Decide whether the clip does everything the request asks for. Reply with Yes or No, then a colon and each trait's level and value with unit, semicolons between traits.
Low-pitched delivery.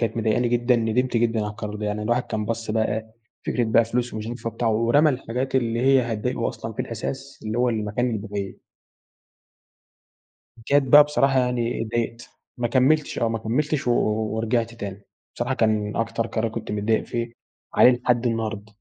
Yes: low, 115 Hz